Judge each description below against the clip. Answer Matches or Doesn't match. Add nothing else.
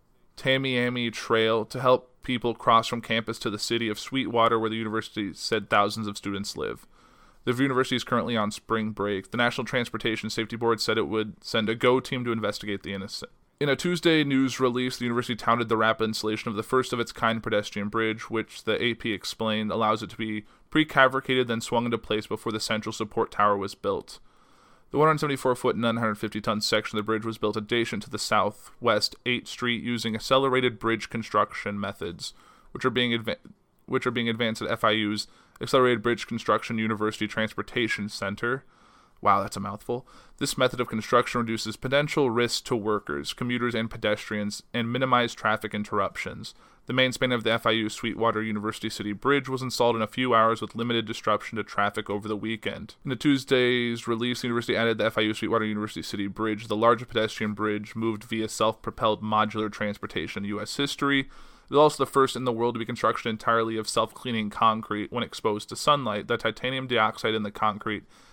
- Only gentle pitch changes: Matches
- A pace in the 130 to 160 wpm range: Doesn't match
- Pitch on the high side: Doesn't match